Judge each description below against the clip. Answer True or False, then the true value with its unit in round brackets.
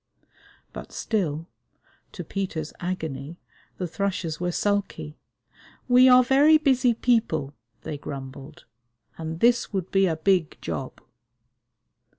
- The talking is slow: True (115 wpm)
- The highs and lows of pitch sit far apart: True (6.7 semitones)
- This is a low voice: False (180 Hz)